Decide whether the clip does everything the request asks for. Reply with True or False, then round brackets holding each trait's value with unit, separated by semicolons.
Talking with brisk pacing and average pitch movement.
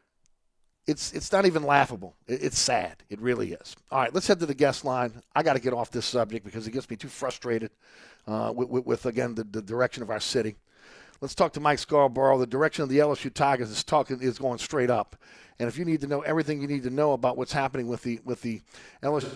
True (240 wpm; 3.3 semitones)